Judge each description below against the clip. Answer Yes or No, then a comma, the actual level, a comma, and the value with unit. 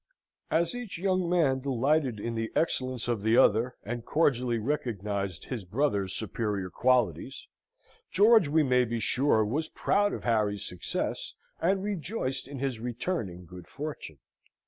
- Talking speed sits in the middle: Yes, average, 145 wpm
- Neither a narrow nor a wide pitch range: No, wide, 6.0 semitones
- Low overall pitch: Yes, low, 125 Hz